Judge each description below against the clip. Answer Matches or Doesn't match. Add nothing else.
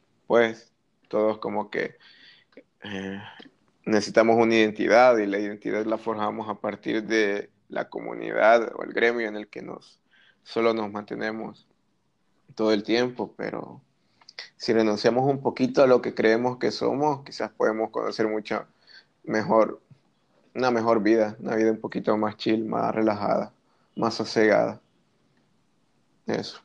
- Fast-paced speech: Doesn't match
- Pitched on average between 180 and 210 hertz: Doesn't match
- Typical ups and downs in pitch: Doesn't match